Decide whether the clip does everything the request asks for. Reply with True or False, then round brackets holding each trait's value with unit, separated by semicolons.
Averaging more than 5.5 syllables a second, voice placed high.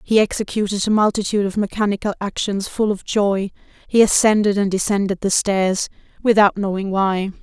False (5.4 syllables/s; 200 Hz)